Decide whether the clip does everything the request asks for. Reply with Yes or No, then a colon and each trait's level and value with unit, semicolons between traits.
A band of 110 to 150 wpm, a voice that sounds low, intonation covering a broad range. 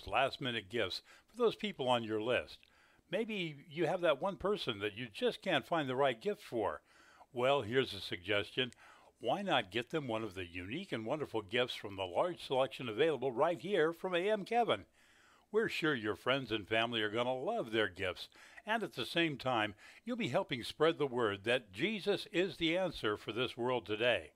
No: average, 200 wpm; low, 130 Hz; wide, 8.0 semitones